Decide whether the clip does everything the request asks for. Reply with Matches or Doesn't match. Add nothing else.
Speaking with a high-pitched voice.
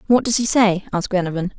Matches